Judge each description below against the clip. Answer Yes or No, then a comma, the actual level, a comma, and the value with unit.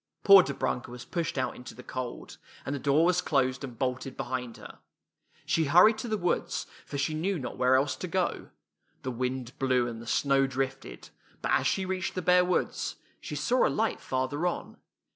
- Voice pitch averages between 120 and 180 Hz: Yes, low, 135 Hz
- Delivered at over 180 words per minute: Yes, average, 200 wpm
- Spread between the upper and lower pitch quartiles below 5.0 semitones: No, wide, 5.6 semitones